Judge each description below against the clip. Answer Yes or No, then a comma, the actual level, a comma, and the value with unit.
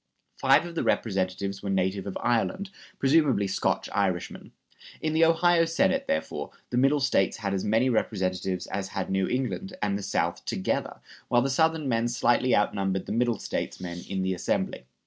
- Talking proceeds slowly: No, average, 175 wpm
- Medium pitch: No, low, 110 Hz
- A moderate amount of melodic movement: No, wide, 6.3 semitones